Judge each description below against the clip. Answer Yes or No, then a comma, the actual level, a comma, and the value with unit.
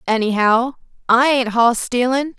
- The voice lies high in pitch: Yes, high, 245 Hz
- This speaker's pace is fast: No, slow, 125 wpm